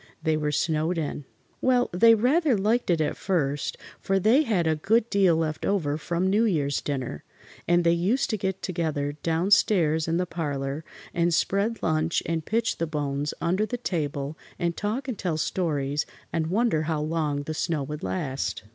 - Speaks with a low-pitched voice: No, medium, 165 Hz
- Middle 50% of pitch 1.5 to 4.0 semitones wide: No, average, 4.7 semitones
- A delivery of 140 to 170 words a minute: No, average, 180 wpm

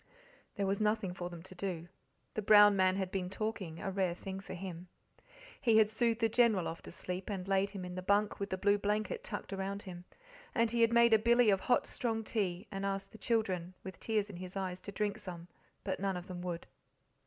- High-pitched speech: Yes, high, 195 Hz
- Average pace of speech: No, fast, 230 wpm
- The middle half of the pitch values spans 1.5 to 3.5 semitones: Yes, average, 2.7 semitones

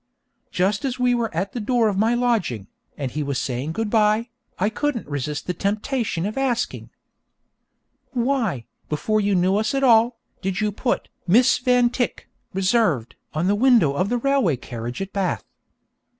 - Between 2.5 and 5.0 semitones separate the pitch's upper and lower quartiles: No, wide, 5.5 semitones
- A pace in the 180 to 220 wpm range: No, average, 170 wpm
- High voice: Yes, high, 210 Hz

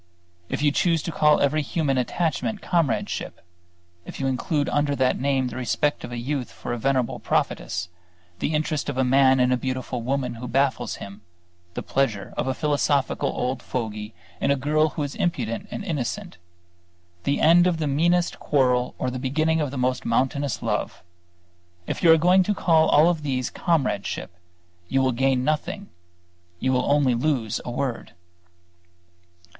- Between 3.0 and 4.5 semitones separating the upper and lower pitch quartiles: Yes, average, 3.4 semitones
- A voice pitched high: No, low, 135 Hz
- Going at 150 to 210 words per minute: Yes, average, 170 wpm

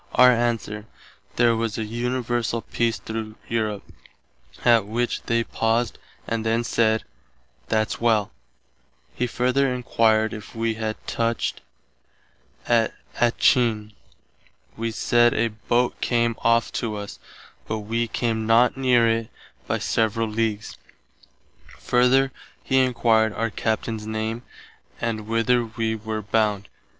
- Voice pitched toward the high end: No, low, 115 Hz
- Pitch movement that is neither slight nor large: No, narrow, 1.3 semitones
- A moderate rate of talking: No, slow, 120 wpm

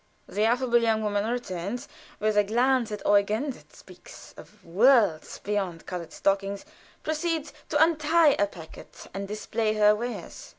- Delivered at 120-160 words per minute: Yes, average, 155 wpm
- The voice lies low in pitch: No, high, 215 Hz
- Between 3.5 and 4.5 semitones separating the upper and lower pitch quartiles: Yes, average, 3.8 semitones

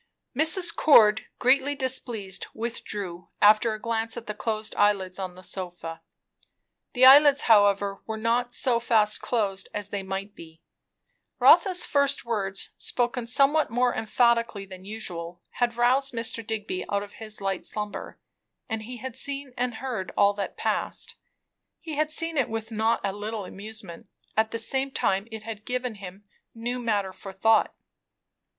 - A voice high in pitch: Yes, high, 220 Hz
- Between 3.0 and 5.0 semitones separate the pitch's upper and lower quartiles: Yes, average, 3.6 semitones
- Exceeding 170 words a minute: No, average, 155 wpm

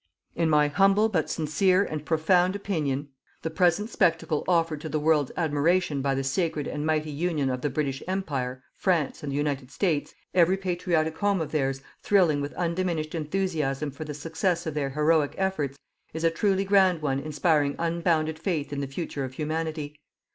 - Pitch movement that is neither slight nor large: Yes, average, 3.4 semitones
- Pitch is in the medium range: Yes, medium, 155 Hz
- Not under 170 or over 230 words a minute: Yes, average, 175 wpm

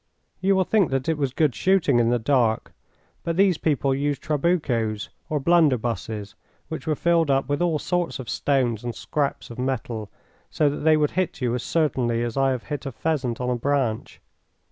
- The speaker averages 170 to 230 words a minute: Yes, average, 195 wpm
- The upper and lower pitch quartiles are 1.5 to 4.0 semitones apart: No, average, 4.7 semitones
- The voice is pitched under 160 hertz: Yes, medium, 140 Hz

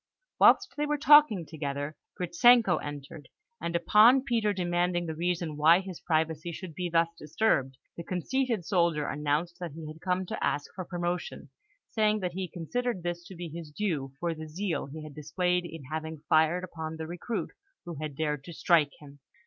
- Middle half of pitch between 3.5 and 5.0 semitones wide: No, average, 2.9 semitones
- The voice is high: No, medium, 170 Hz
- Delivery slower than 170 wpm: No, average, 180 wpm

